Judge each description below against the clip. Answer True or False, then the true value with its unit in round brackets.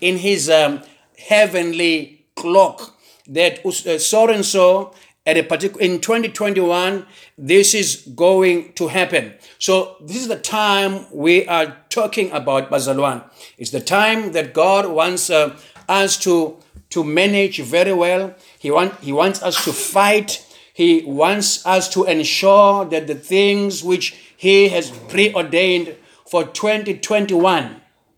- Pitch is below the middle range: False (185 Hz)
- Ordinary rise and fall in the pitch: True (3.7 semitones)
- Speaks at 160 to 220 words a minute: False (135 wpm)